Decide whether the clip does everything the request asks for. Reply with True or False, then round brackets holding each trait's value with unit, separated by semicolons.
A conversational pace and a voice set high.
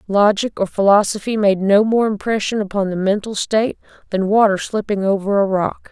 True (170 wpm; 205 Hz)